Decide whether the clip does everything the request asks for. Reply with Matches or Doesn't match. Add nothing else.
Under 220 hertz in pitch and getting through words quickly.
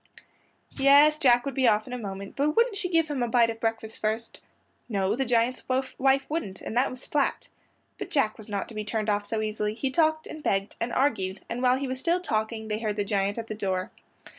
Doesn't match